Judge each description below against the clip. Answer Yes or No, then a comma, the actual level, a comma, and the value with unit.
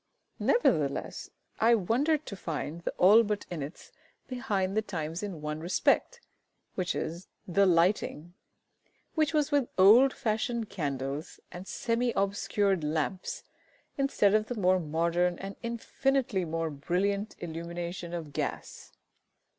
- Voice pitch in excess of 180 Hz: Yes, high, 190 Hz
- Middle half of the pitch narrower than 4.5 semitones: No, average, 5.2 semitones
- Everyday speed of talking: No, slow, 120 wpm